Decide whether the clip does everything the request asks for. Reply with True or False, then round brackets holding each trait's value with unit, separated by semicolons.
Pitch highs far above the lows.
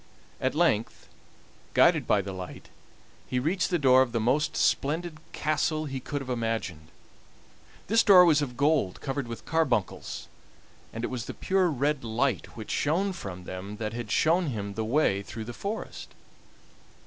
True (5.8 semitones)